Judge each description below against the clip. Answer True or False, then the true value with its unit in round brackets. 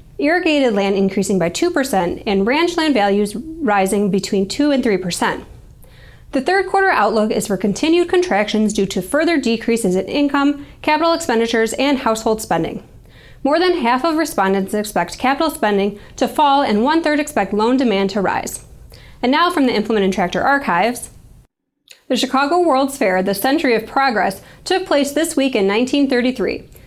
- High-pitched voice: True (245 Hz)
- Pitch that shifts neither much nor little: False (6.4 semitones)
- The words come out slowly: False (160 wpm)